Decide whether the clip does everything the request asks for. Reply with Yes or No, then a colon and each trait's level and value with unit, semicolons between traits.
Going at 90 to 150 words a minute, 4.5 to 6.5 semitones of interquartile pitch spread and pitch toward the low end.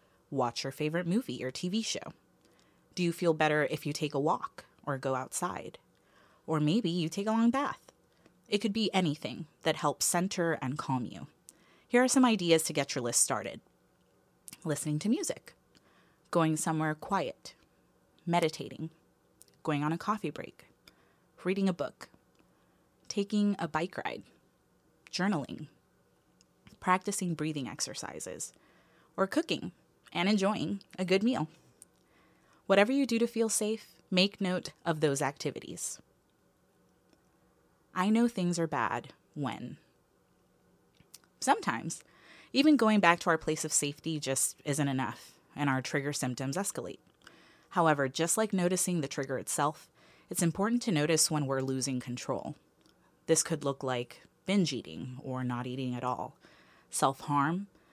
No: average, 140 wpm; wide, 5.4 semitones; medium, 160 Hz